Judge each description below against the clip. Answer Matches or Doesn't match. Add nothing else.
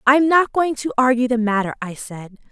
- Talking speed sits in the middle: Doesn't match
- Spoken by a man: Doesn't match